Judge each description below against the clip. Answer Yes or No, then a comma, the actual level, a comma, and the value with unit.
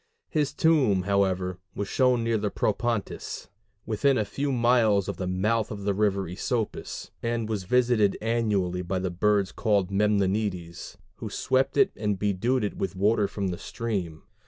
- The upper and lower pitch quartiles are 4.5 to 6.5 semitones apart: No, average, 3.4 semitones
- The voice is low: Yes, low, 105 Hz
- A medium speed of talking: Yes, average, 160 wpm